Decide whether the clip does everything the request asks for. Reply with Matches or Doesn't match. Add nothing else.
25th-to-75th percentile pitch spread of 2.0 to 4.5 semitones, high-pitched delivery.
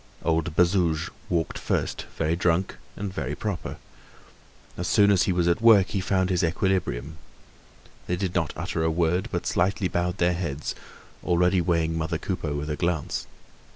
Doesn't match